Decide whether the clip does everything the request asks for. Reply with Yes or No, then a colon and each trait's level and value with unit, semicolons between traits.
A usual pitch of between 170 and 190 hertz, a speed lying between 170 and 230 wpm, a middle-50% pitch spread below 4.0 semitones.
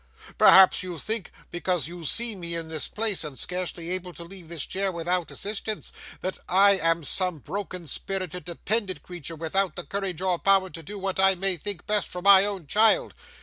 Yes: medium, 185 Hz; average, 190 wpm; narrow, 2.5 semitones